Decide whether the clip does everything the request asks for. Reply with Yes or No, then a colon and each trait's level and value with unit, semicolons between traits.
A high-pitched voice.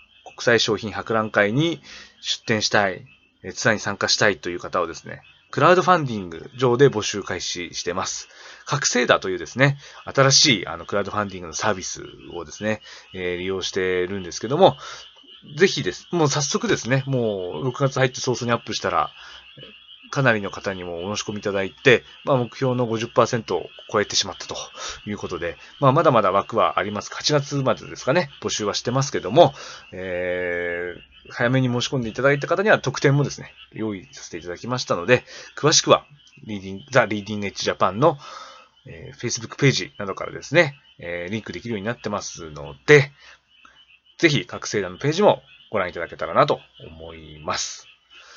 No: low, 115 Hz